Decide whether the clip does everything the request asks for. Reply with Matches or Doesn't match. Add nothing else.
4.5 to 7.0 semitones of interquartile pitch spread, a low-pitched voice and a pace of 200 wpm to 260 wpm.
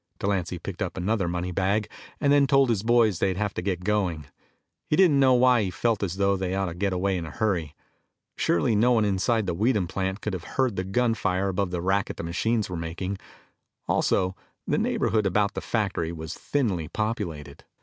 Doesn't match